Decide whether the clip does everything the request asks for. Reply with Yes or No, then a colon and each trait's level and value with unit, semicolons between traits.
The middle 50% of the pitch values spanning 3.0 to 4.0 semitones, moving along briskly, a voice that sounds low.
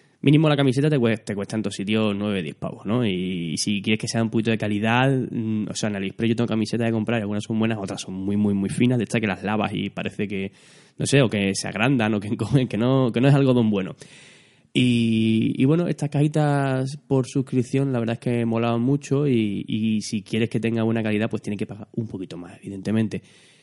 Yes: average, 3.5 semitones; fast, 245 wpm; low, 115 Hz